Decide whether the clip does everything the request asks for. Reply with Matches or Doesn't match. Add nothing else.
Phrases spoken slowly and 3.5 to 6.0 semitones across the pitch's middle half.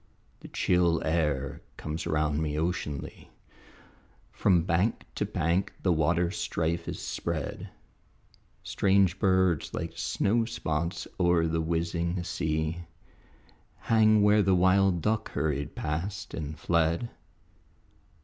Doesn't match